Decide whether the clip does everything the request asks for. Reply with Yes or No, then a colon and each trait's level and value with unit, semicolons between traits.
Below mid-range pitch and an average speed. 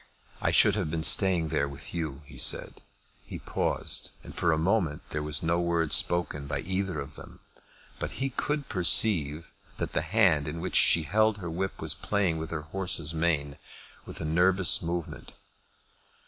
Yes: very low, 85 Hz; average, 175 wpm